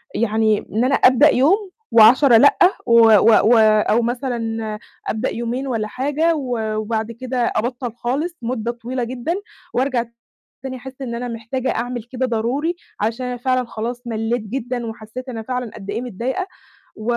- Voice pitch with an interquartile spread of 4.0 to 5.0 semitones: No, narrow, 2.4 semitones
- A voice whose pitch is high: Yes, high, 240 Hz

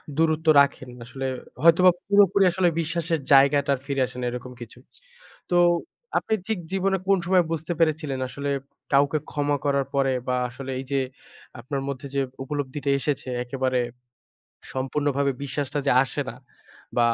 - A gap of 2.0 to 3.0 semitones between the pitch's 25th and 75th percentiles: No, average, 3.4 semitones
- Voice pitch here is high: No, medium, 140 Hz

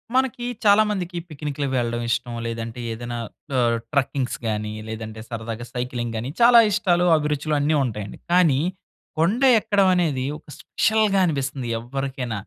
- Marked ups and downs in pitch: Yes, wide, 6.7 semitones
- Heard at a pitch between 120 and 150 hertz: Yes, low, 135 Hz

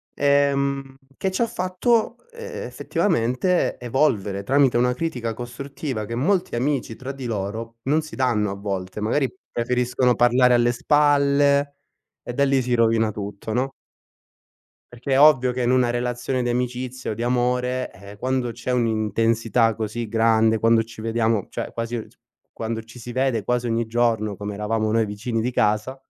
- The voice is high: No, low, 120 Hz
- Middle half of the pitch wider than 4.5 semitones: No, average, 2.9 semitones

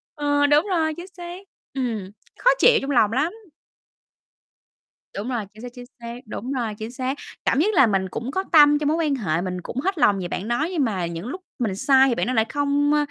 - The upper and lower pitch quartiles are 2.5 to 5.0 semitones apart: No, wide, 5.4 semitones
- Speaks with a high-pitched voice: Yes, very high, 265 Hz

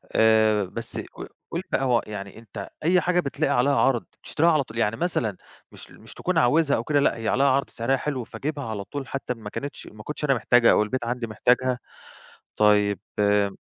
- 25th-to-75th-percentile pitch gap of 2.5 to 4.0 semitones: No, average, 4.6 semitones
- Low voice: Yes, low, 120 Hz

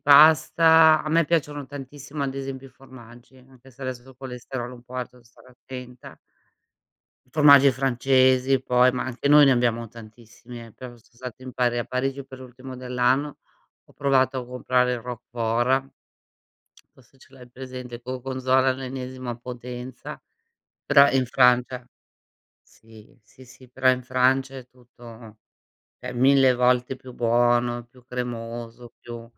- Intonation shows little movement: Yes, narrow, 1.6 semitones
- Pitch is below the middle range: Yes, low, 125 Hz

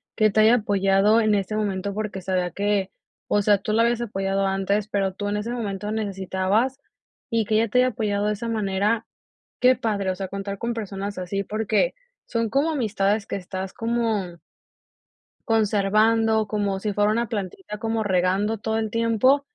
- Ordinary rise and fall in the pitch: No, narrow, 2.3 semitones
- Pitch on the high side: Yes, high, 210 Hz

